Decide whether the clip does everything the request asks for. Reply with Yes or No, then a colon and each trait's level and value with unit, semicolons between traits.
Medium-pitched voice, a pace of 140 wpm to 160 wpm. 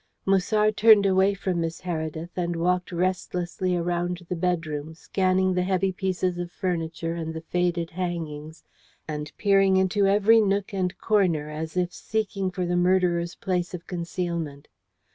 Yes: medium, 180 Hz; average, 150 wpm